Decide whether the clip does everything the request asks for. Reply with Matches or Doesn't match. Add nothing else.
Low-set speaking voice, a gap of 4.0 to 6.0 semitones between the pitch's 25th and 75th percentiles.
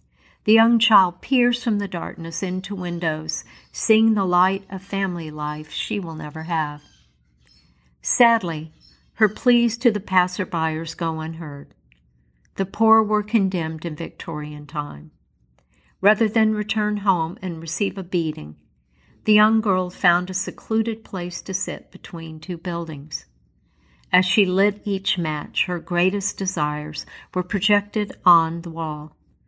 Doesn't match